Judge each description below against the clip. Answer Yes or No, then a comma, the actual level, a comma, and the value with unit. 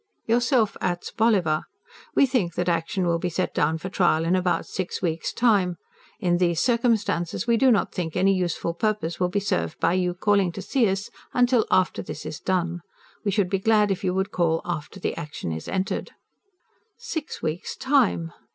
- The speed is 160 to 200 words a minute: Yes, average, 185 wpm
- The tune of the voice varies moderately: Yes, average, 3.8 semitones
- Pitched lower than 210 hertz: Yes, medium, 185 Hz